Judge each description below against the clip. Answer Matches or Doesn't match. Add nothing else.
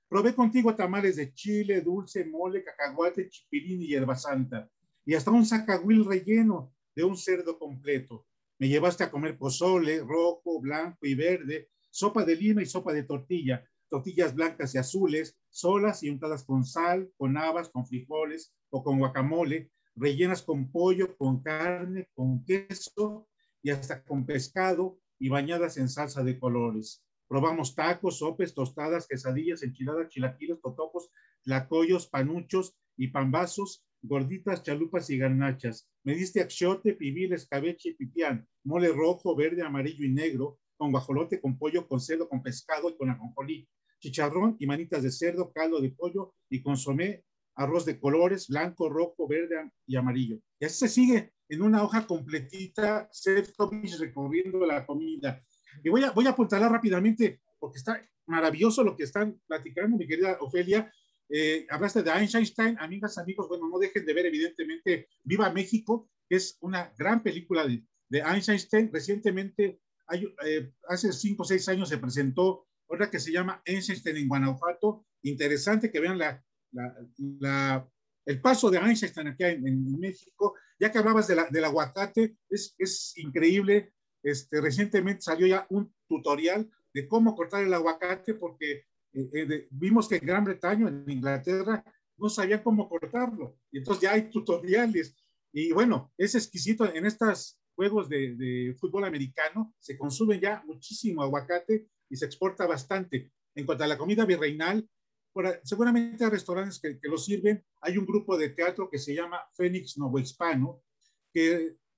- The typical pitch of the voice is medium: Matches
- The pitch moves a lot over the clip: Matches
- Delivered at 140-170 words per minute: Matches